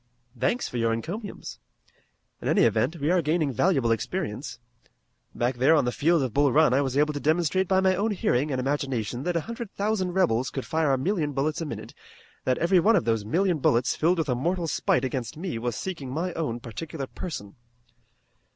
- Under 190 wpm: No, fast, 205 wpm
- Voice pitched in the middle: Yes, medium, 150 Hz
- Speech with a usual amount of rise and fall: No, wide, 5.7 semitones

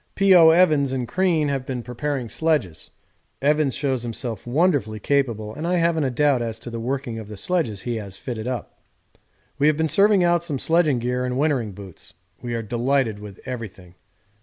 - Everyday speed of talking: Yes, average, 185 wpm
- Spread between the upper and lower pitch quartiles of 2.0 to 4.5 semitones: No, average, 5.1 semitones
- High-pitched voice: No, low, 130 Hz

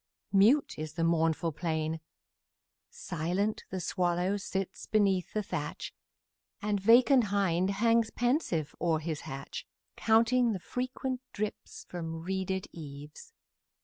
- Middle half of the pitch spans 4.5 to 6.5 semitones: Yes, average, 5.1 semitones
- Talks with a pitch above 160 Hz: Yes, high, 190 Hz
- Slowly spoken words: Yes, slow, 115 wpm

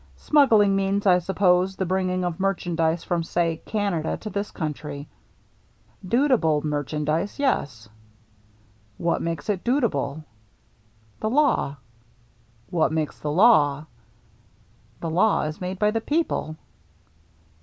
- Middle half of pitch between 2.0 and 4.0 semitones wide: No, wide, 5.4 semitones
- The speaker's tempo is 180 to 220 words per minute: No, average, 140 wpm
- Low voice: No, medium, 170 Hz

